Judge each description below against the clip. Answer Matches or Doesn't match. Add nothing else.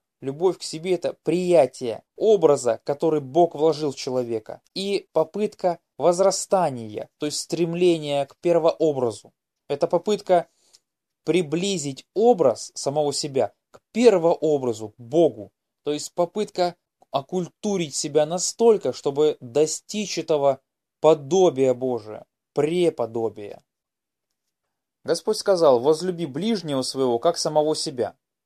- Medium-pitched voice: Matches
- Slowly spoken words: Matches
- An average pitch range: Matches